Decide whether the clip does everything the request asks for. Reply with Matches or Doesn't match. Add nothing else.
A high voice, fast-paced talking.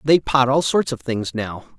Doesn't match